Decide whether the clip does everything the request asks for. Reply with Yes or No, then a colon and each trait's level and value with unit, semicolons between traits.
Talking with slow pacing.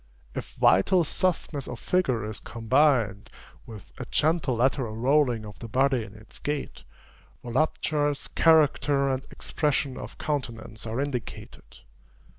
Yes: slow, 125 wpm